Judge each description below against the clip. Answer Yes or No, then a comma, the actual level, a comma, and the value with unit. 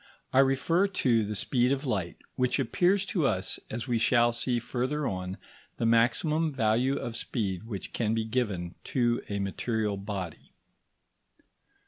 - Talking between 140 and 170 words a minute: Yes, average, 150 wpm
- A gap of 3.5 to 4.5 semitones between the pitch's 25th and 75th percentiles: Yes, average, 4.0 semitones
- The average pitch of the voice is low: Yes, low, 120 Hz